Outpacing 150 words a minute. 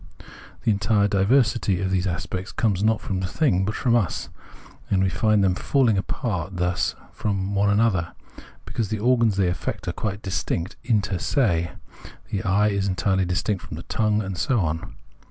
Yes: average, 180 wpm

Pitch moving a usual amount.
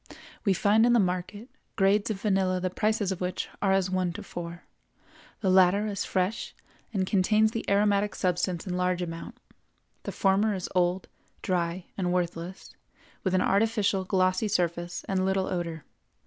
No: narrow, 2.1 semitones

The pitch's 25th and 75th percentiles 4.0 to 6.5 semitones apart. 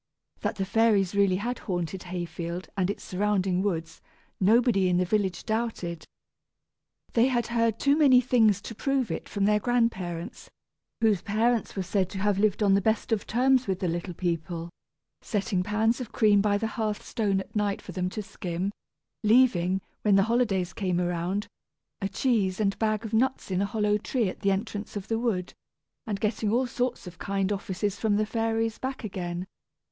No: average, 3.3 semitones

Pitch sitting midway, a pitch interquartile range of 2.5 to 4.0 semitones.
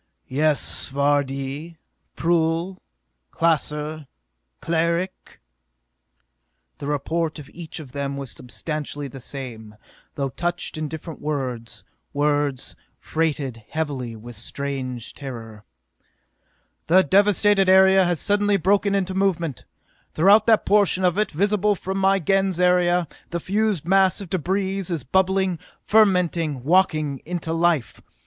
No: medium, 165 Hz; average, 5.1 semitones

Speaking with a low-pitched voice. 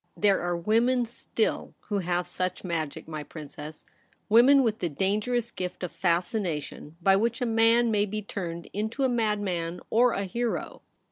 No: high, 205 Hz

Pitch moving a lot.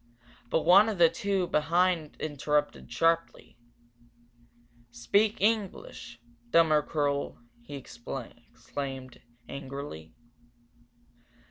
No: average, 4.4 semitones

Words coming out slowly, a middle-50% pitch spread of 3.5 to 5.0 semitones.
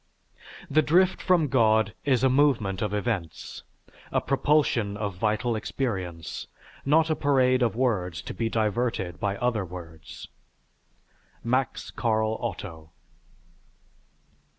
Yes: slow, 115 wpm; average, 4.7 semitones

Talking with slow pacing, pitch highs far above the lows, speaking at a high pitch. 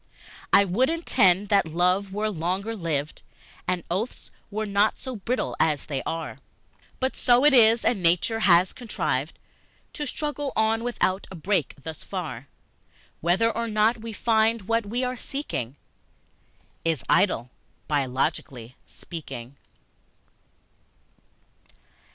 Yes: slow, 125 wpm; wide, 5.7 semitones; high, 200 Hz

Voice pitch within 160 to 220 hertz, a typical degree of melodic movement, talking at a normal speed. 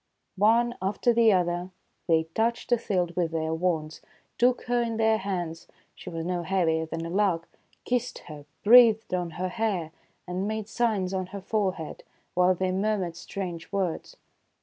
Yes: medium, 185 Hz; average, 4.3 semitones; average, 170 wpm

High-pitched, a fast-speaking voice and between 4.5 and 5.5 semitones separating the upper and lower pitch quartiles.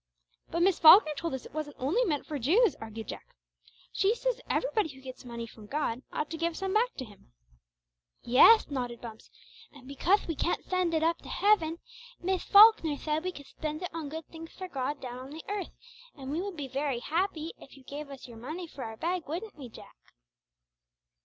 Yes: very high, 310 Hz; fast, 210 wpm; average, 5.2 semitones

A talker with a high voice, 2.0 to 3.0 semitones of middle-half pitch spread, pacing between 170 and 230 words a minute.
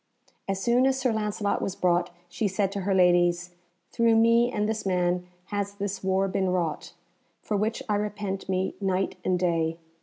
Yes: high, 195 Hz; narrow, 2.6 semitones; average, 180 wpm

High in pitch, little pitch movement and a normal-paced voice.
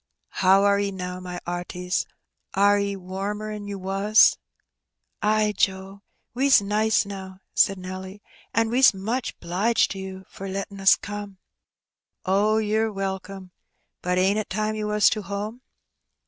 Yes: high, 200 Hz; narrow, 1.9 semitones; average, 155 wpm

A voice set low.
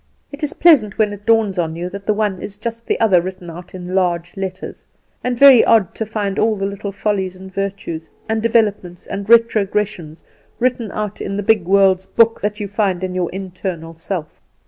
No: high, 200 Hz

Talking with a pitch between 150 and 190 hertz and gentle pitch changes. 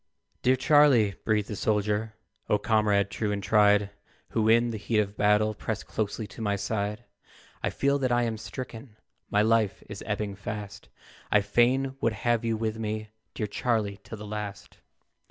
No: low, 110 Hz; narrow, 1.8 semitones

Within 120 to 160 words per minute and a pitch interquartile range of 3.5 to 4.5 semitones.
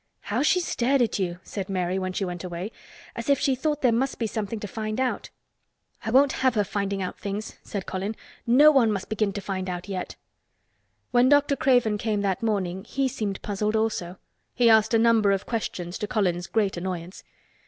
No: average, 200 wpm; average, 3.8 semitones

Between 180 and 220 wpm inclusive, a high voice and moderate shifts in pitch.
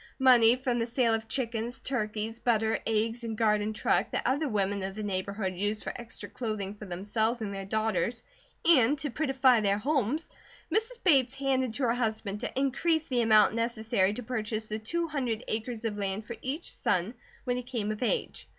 Yes: average, 190 wpm; high, 225 Hz; average, 3.3 semitones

